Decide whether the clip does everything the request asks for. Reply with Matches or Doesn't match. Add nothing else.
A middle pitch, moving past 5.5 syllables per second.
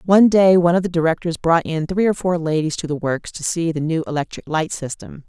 Matches